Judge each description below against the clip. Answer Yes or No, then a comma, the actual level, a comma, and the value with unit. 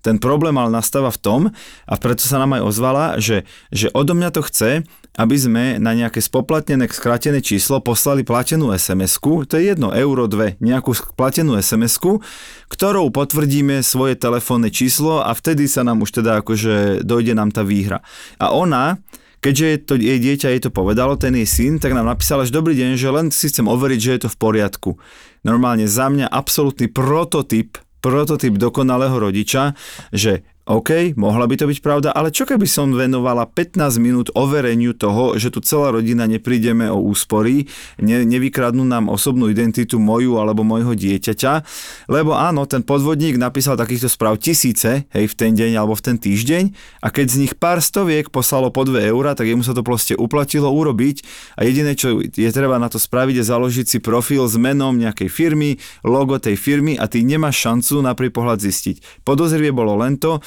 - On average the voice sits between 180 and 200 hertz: No, low, 125 Hz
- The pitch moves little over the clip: No, average, 3.9 semitones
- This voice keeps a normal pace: No, fast, 185 wpm